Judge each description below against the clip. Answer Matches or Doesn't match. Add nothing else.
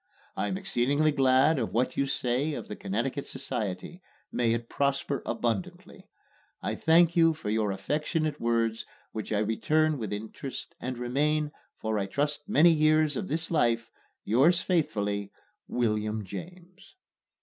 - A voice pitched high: Doesn't match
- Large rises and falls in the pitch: Matches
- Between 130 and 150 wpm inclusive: Matches